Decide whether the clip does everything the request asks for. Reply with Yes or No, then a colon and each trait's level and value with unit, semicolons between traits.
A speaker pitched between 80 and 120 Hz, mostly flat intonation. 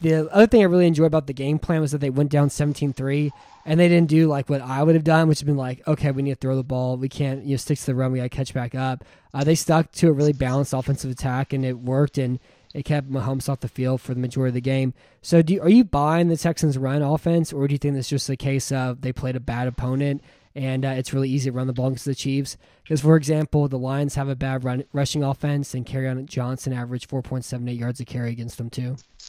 No: low, 135 Hz; narrow, 2.3 semitones